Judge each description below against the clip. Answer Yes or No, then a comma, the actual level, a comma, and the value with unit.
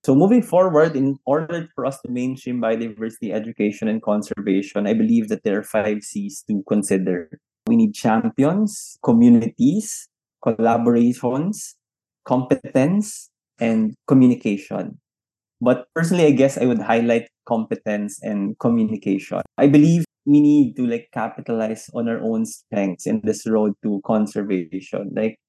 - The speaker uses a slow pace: No, average, 135 wpm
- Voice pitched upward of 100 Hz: Yes, low, 120 Hz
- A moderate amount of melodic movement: No, wide, 7.1 semitones